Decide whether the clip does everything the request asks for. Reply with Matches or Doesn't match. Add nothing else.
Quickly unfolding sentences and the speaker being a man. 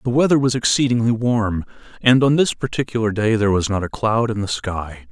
Matches